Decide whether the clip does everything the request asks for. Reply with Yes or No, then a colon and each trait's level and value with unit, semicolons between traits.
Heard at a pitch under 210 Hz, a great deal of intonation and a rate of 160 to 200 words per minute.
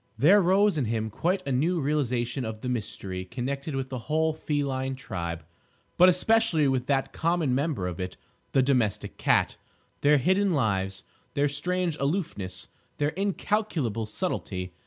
No: medium, 140 Hz; wide, 6.7 semitones; average, 145 wpm